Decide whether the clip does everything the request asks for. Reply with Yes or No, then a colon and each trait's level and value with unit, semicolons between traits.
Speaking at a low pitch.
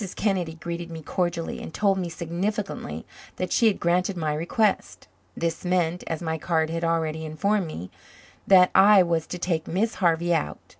No: medium, 170 Hz